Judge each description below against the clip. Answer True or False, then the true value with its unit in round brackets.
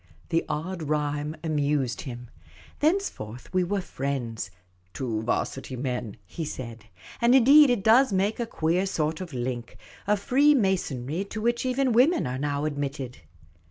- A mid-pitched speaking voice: True (155 Hz)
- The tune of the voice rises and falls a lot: True (8.5 semitones)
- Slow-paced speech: False (160 wpm)